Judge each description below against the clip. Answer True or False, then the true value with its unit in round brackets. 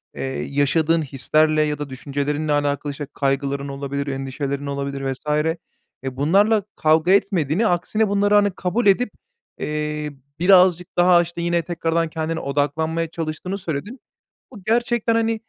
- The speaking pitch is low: False (160 Hz)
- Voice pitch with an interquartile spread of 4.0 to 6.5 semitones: True (4.3 semitones)